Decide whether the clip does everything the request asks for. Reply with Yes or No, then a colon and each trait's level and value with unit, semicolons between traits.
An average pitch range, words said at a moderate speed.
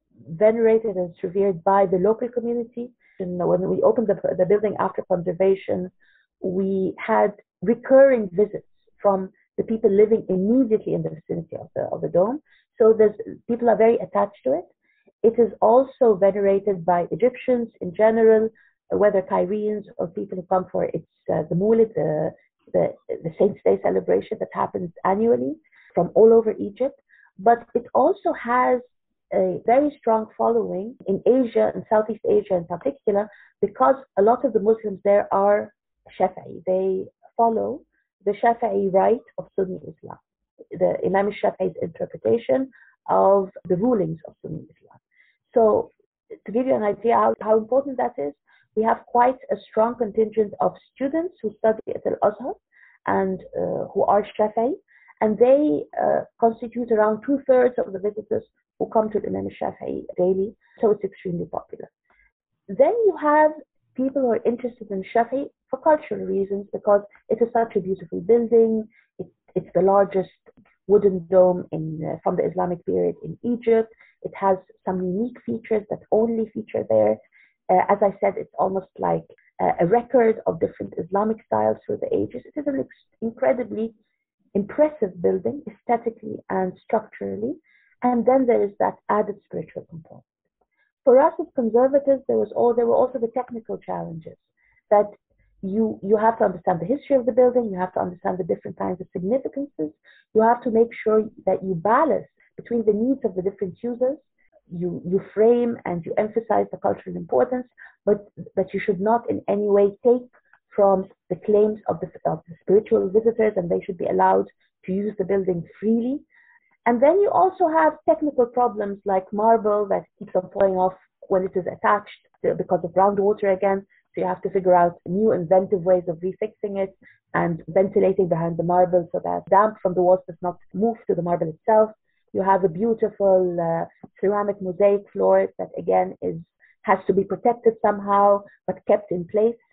Yes: average, 4.0 semitones; average, 170 wpm